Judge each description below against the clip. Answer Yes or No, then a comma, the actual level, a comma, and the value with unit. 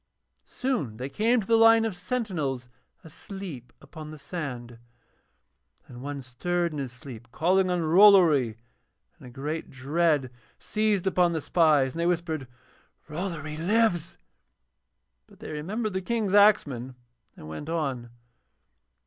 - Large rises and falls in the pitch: Yes, wide, 5.9 semitones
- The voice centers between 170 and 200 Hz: No, medium, 160 Hz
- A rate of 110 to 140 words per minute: Yes, slow, 135 wpm